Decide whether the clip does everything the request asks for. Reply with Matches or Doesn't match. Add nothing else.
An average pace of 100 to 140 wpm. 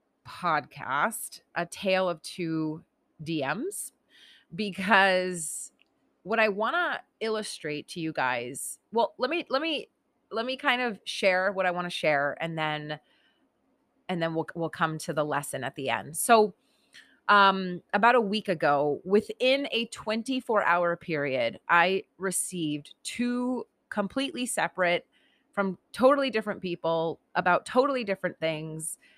Matches